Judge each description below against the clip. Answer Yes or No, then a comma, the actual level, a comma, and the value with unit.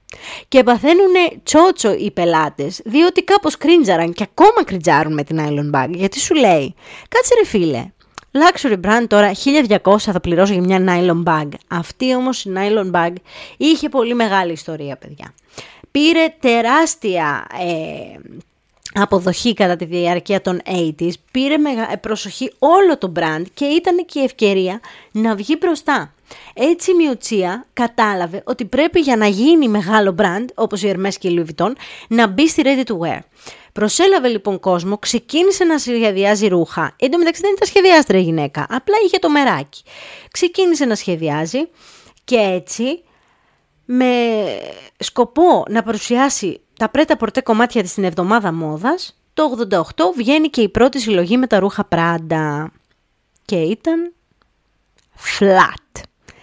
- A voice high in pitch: Yes, high, 225 Hz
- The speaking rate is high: No, average, 145 wpm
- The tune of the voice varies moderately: No, wide, 8.2 semitones